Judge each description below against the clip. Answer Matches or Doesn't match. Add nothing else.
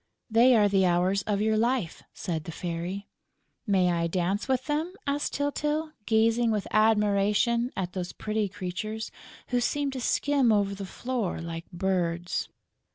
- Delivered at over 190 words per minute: Doesn't match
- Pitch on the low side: Doesn't match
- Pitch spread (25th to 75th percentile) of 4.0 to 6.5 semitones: Matches